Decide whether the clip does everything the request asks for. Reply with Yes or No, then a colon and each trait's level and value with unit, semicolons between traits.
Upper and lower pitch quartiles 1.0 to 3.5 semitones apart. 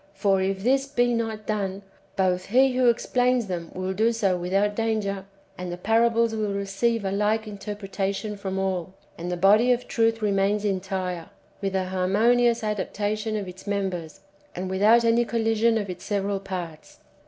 Yes: average, 2.9 semitones